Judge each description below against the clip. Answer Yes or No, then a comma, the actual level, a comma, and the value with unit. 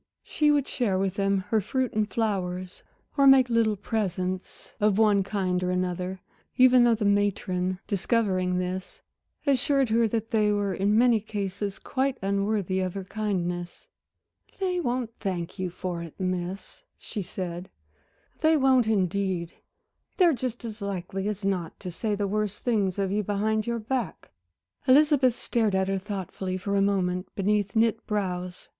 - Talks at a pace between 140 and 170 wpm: Yes, average, 160 wpm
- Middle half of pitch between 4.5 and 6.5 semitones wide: No, average, 3.3 semitones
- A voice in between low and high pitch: No, high, 200 Hz